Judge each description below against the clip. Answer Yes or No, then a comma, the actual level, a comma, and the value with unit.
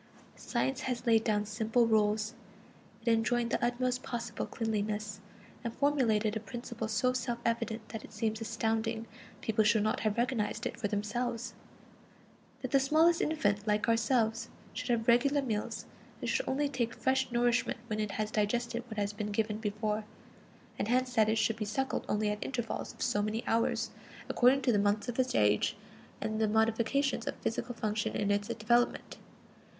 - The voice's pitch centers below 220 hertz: No, high, 225 Hz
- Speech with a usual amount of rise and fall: No, narrow, 2.2 semitones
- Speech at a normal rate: Yes, average, 170 wpm